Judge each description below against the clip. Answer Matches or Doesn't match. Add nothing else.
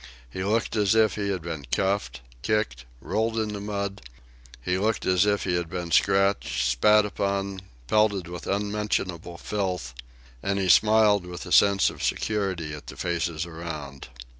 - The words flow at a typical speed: Matches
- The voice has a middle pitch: Doesn't match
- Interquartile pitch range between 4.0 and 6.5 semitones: Doesn't match